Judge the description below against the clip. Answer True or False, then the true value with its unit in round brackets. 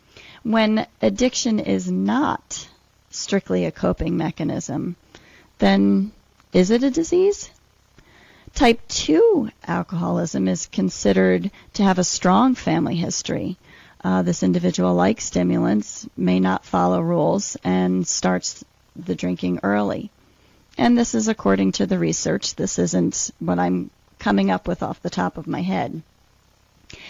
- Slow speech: True (130 wpm)